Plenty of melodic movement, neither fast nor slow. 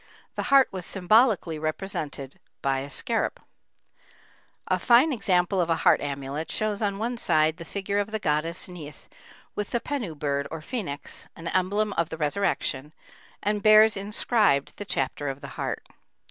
Yes: wide, 5.8 semitones; average, 160 wpm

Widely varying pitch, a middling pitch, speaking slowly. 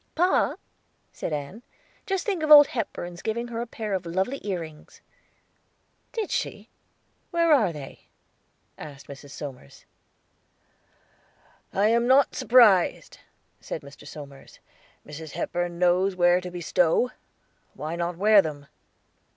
Yes: wide, 7.0 semitones; medium, 180 Hz; slow, 125 wpm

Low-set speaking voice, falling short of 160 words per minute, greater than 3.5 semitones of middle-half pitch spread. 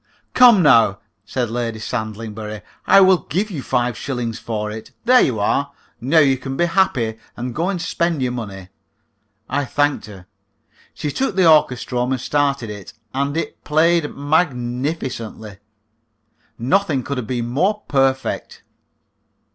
Yes: low, 130 Hz; average, 145 wpm; wide, 5.4 semitones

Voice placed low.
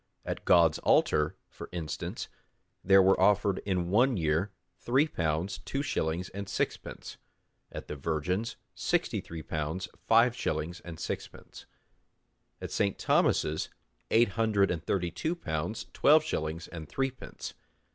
Yes: very low, 95 Hz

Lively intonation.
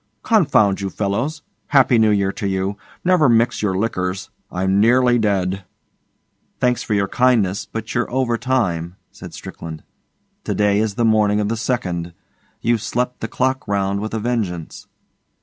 No: average, 3.8 semitones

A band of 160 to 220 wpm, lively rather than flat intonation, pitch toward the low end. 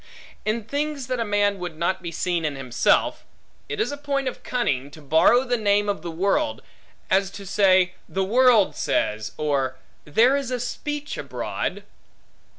No: average, 170 wpm; wide, 6.9 semitones; high, 200 Hz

